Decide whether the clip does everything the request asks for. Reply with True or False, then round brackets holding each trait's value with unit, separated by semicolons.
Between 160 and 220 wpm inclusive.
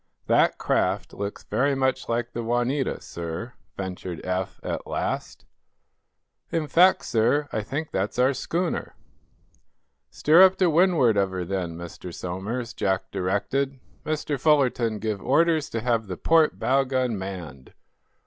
False (140 wpm)